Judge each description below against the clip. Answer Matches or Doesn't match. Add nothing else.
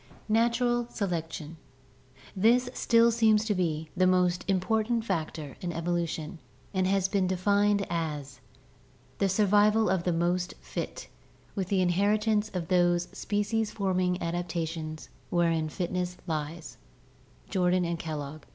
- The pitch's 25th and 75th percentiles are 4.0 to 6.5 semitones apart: Doesn't match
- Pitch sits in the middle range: Matches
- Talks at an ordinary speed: Doesn't match